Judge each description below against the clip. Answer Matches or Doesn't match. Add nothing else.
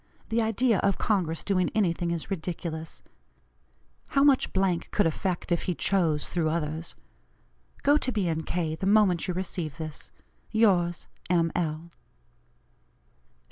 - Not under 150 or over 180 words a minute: Doesn't match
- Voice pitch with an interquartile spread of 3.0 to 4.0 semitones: Matches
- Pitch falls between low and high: Matches